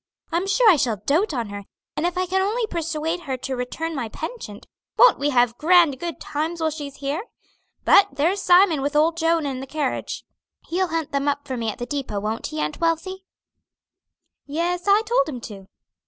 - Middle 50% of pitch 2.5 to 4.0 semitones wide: No, average, 4.8 semitones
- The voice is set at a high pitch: Yes, very high, 310 Hz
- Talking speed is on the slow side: No, average, 200 wpm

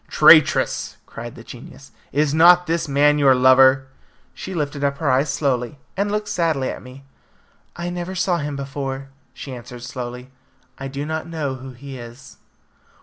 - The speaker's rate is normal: Yes, average, 165 wpm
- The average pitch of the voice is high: No, medium, 140 Hz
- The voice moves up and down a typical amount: Yes, average, 3.4 semitones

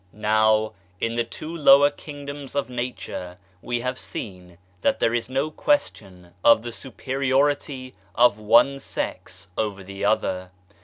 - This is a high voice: No, low, 120 Hz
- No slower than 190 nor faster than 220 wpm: No, average, 140 wpm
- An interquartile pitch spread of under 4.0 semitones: No, average, 4.5 semitones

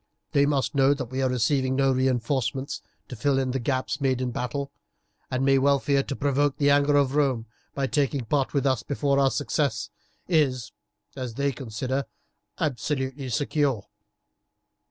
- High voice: No, low, 135 Hz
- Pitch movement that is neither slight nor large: No, narrow, 1.7 semitones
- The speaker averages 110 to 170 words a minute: Yes, average, 160 wpm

